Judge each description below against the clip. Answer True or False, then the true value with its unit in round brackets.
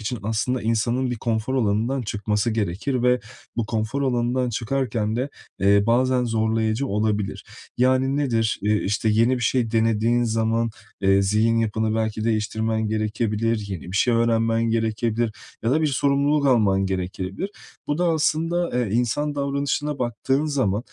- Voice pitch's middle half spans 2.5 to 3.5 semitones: True (3.0 semitones)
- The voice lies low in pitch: True (115 Hz)